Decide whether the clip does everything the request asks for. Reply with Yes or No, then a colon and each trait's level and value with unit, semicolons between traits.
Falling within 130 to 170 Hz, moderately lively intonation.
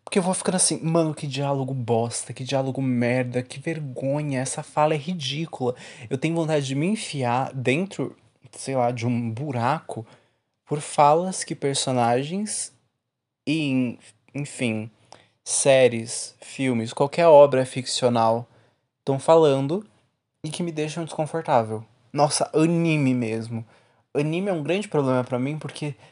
Yes: low, 135 Hz; average, 4.1 semitones